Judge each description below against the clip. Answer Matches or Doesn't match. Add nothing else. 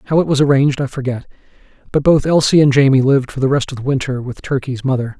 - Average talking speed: Doesn't match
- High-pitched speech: Doesn't match